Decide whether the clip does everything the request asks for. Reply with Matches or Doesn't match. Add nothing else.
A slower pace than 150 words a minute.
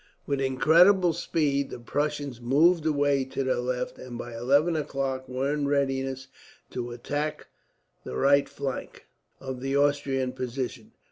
Matches